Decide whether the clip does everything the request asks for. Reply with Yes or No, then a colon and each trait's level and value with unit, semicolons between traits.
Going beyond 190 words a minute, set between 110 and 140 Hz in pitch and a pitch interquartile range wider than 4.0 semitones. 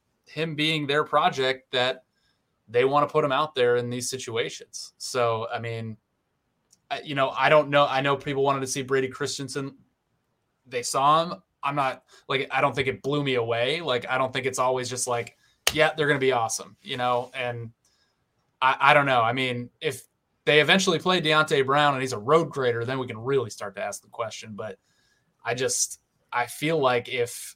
No: fast, 205 wpm; low, 135 Hz; average, 3.1 semitones